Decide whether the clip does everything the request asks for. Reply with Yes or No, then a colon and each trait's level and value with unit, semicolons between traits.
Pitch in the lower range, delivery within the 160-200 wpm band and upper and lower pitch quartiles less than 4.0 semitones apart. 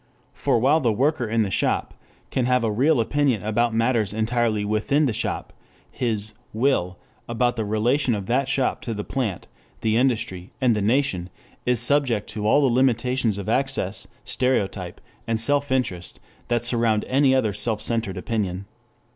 Yes: low, 115 Hz; average, 165 wpm; average, 3.5 semitones